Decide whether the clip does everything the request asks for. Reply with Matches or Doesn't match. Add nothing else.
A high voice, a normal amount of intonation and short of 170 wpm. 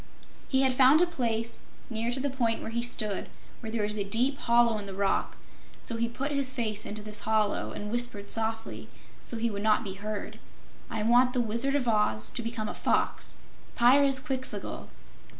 Doesn't match